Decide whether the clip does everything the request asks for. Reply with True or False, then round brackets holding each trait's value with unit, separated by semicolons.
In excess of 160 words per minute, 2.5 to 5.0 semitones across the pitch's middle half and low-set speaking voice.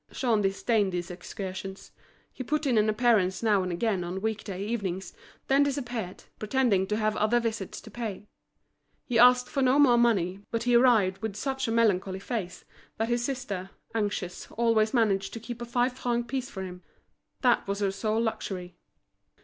False (180 wpm; 3.8 semitones; 220 Hz)